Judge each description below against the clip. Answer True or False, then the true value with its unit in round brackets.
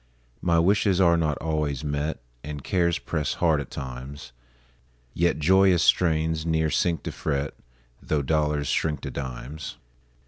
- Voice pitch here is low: True (80 Hz)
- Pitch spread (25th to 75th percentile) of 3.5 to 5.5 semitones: False (2.8 semitones)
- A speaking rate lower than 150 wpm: True (140 wpm)